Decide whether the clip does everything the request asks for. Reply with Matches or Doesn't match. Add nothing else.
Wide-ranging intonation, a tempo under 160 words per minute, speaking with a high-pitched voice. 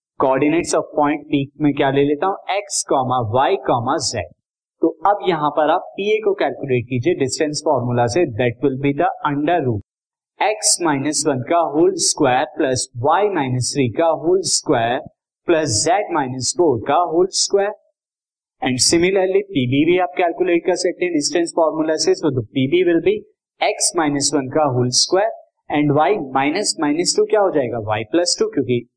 Doesn't match